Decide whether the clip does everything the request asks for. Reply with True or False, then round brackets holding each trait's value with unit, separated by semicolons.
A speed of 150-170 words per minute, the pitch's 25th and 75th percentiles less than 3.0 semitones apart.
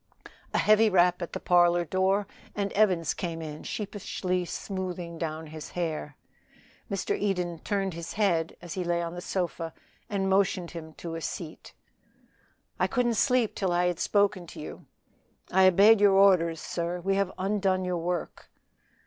True (165 wpm; 2.6 semitones)